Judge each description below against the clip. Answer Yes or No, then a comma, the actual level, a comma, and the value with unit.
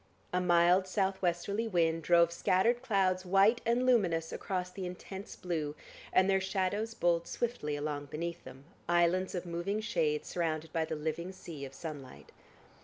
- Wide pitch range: No, average, 2.9 semitones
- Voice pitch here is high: No, medium, 175 Hz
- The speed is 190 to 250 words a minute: No, average, 160 wpm